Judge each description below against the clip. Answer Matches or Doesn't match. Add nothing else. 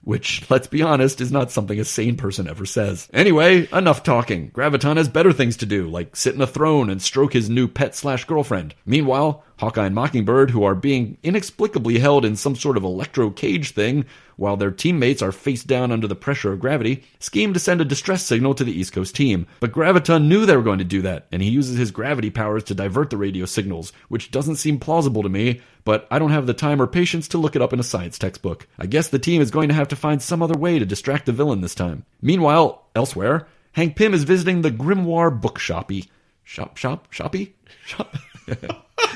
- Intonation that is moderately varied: Doesn't match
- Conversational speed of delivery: Doesn't match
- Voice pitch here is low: Matches